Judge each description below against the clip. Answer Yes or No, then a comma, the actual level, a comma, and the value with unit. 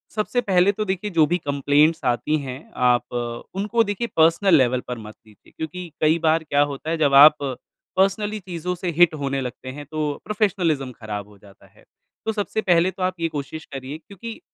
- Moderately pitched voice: Yes, medium, 160 Hz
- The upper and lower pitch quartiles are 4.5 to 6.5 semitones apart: Yes, wide, 5.6 semitones